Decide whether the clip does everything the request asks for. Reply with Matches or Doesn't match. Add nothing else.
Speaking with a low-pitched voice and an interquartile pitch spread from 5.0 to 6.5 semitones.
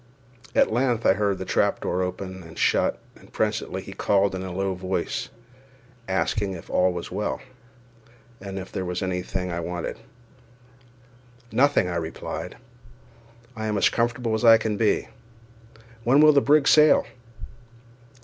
Doesn't match